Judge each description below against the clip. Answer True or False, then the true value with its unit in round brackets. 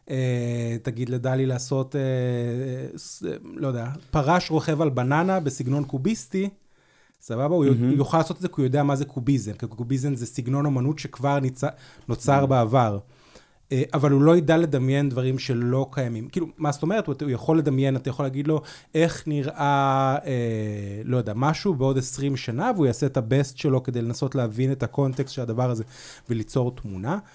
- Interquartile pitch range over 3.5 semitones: False (2.5 semitones)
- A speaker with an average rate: False (160 wpm)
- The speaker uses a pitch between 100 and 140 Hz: True (135 Hz)